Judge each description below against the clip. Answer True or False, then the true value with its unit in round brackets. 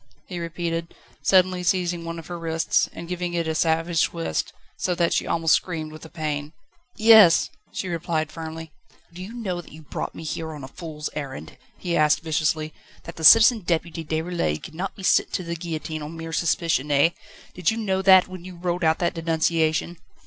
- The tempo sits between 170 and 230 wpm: True (195 wpm)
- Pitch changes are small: True (2.0 semitones)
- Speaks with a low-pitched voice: False (165 Hz)